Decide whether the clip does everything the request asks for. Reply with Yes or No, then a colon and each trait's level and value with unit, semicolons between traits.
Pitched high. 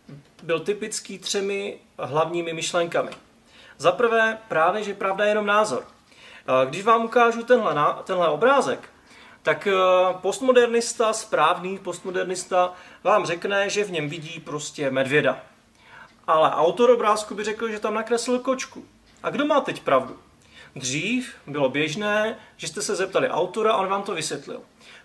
Yes: high, 200 Hz